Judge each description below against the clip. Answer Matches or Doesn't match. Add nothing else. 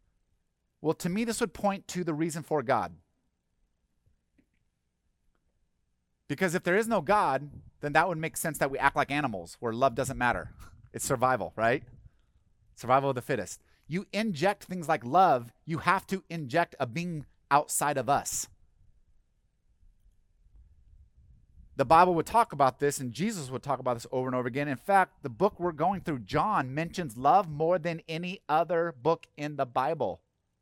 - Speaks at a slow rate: Doesn't match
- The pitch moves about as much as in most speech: Doesn't match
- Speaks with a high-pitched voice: Doesn't match